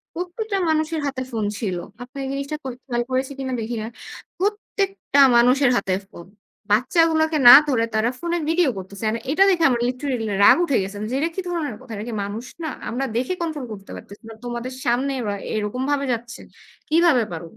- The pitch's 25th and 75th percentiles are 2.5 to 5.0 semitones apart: No, wide, 5.5 semitones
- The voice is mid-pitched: No, very high, 255 Hz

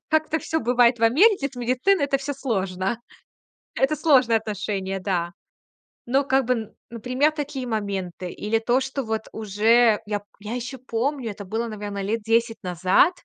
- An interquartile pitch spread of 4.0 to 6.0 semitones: Yes, average, 4.4 semitones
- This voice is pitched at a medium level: No, high, 230 Hz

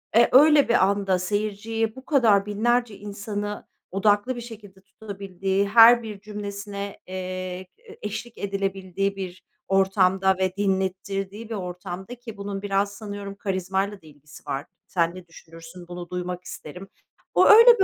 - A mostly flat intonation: Yes, narrow, 2.2 semitones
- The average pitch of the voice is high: Yes, high, 200 Hz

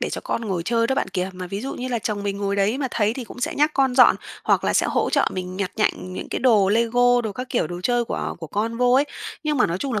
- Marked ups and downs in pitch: No, average, 4.0 semitones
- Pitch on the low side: No, high, 225 Hz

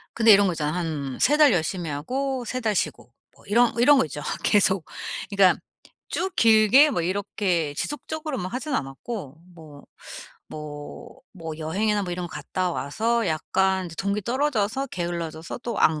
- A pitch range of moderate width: No, wide, 6.4 semitones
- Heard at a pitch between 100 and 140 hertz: No, high, 190 Hz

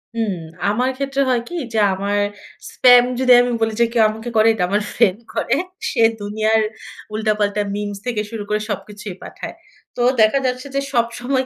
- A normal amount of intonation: Yes, average, 3.0 semitones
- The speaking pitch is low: No, high, 220 Hz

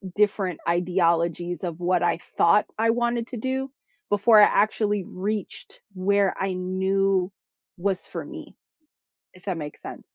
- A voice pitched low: No, high, 190 Hz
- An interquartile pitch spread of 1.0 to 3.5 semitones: Yes, average, 2.8 semitones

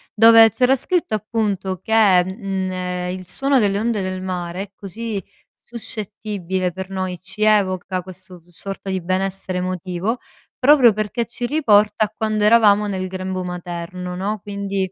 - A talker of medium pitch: No, high, 195 Hz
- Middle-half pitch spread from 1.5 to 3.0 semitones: Yes, narrow, 2.6 semitones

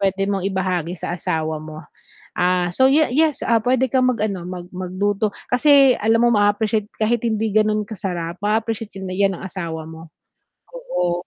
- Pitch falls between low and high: No, high, 200 Hz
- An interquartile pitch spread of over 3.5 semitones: Yes, average, 4.0 semitones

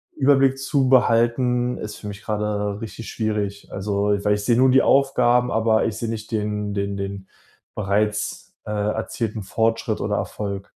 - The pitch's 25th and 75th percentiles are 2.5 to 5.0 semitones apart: Yes, average, 2.9 semitones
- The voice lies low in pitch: Yes, low, 110 Hz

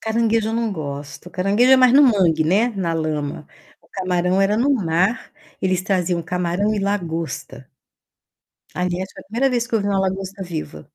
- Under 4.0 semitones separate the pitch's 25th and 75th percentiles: No, average, 4.3 semitones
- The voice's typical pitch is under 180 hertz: No, high, 190 Hz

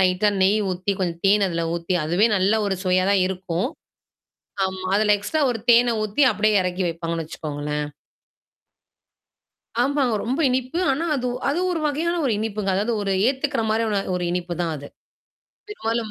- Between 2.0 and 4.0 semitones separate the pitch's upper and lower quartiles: No, average, 4.6 semitones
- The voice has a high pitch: Yes, high, 200 Hz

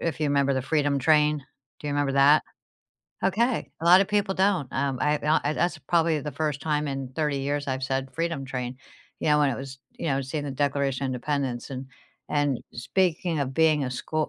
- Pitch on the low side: No, medium, 145 Hz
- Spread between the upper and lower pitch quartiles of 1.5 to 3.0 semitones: Yes, narrow, 2.6 semitones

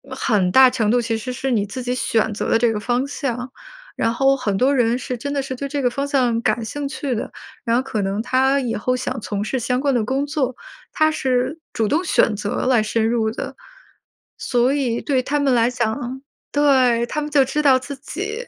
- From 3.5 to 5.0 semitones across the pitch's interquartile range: No, average, 3.1 semitones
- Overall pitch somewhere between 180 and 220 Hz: No, very high, 255 Hz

